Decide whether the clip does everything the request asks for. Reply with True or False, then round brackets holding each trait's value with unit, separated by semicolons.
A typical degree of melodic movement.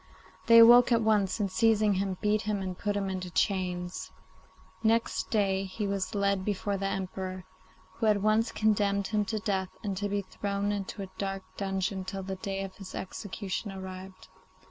False (1.7 semitones)